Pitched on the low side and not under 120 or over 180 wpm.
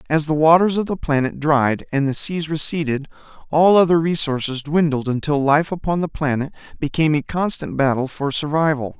No: medium, 150 Hz; average, 175 wpm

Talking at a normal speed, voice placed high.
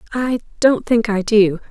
Yes: average, 175 wpm; high, 220 Hz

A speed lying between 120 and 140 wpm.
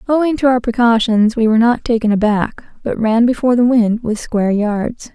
No: average, 200 wpm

